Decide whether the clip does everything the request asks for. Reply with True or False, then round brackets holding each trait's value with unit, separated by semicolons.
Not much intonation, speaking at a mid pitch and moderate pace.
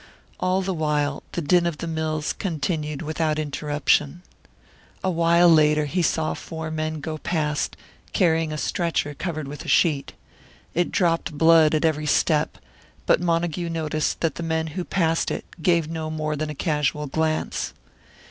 True (1.8 semitones; 160 Hz; 165 wpm)